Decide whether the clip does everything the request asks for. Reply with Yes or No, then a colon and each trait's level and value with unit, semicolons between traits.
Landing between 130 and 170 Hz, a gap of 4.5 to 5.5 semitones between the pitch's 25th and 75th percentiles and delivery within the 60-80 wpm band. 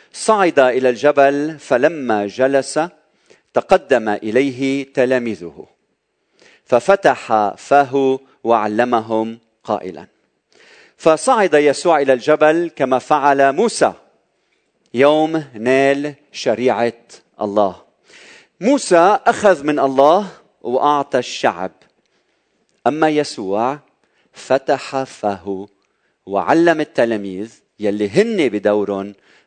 Yes: low, 135 Hz; average, 4.9 semitones; average, 75 wpm